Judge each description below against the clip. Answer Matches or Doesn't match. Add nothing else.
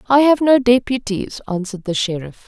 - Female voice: Matches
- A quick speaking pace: Doesn't match